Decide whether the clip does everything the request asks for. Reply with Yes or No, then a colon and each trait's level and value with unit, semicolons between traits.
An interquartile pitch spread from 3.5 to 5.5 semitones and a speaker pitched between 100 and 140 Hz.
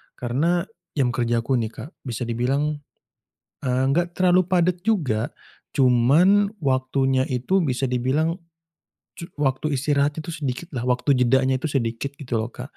Yes: average, 4.4 semitones; low, 135 Hz